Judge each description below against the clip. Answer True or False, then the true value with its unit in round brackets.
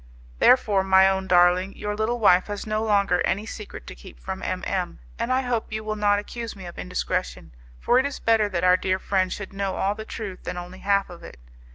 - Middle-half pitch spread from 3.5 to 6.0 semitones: False (2.7 semitones)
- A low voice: False (200 Hz)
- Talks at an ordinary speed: False (230 wpm)